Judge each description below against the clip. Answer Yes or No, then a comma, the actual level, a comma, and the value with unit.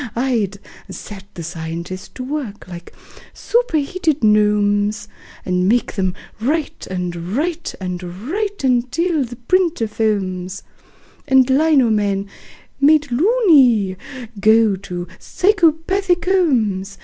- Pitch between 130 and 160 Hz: No, high, 230 Hz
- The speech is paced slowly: Yes, slow, 105 wpm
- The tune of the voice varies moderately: No, wide, 8.1 semitones